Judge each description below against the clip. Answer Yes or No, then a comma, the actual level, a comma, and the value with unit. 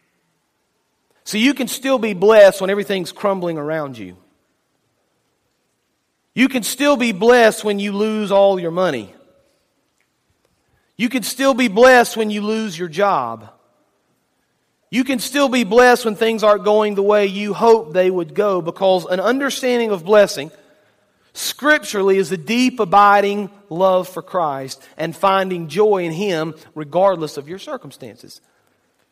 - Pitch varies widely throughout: No, average, 3.8 semitones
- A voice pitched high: Yes, high, 205 Hz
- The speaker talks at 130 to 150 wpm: Yes, average, 145 wpm